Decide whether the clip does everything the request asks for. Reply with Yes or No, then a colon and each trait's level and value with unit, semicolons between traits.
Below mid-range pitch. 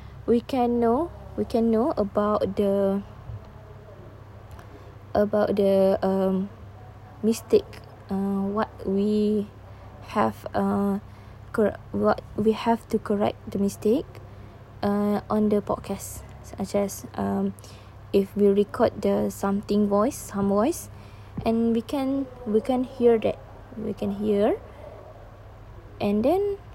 No: high, 195 Hz